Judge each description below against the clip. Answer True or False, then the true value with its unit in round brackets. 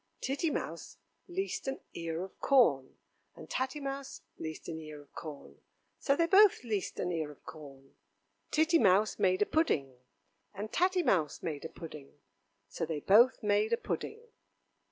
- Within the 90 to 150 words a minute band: False (160 wpm)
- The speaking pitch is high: True (195 Hz)